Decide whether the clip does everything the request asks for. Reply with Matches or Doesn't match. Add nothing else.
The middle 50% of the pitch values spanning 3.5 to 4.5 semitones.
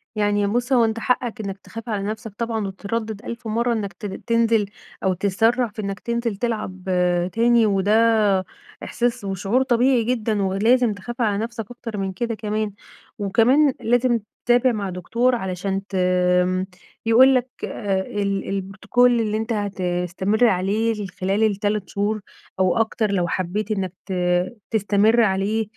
Doesn't match